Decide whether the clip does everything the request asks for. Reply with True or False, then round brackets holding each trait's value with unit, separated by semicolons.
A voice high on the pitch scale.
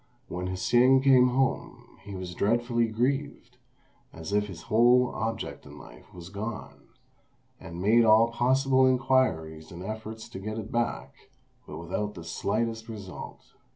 False (110 Hz)